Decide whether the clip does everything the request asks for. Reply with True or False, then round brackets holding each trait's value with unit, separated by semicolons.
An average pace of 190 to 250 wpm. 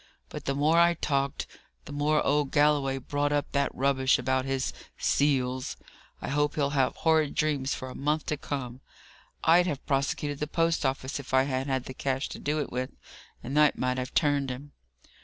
True (195 wpm)